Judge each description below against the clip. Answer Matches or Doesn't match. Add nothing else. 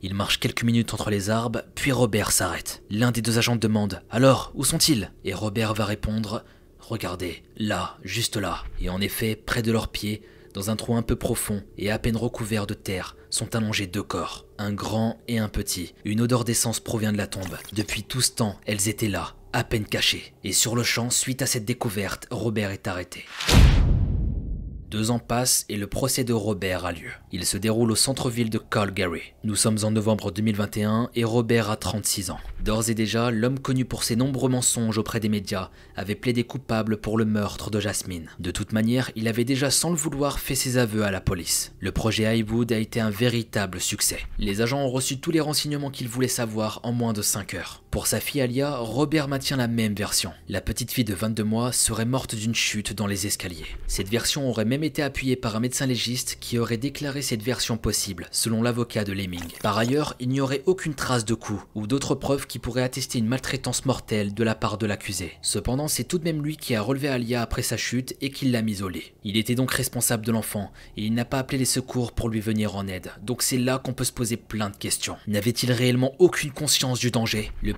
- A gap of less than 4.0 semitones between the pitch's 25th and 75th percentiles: Matches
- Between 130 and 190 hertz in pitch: Doesn't match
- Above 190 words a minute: Matches